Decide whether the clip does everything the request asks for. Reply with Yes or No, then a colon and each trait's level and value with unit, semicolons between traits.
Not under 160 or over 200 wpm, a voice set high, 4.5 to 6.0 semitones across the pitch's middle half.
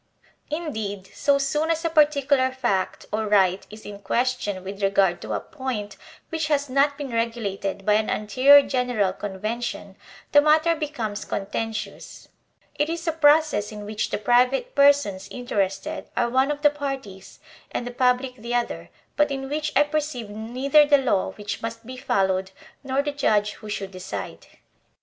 Yes: average, 165 wpm; high, 245 Hz; wide, 5.6 semitones